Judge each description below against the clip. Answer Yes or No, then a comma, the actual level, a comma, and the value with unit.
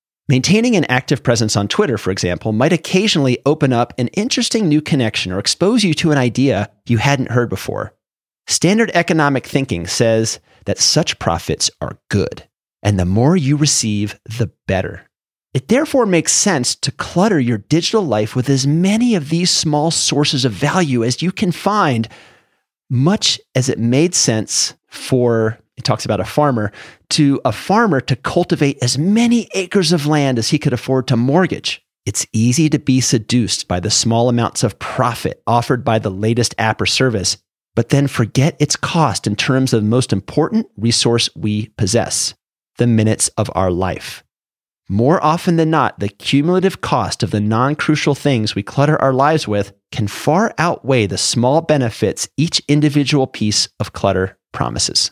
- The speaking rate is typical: Yes, average, 170 wpm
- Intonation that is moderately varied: No, wide, 5.7 semitones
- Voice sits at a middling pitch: No, low, 130 Hz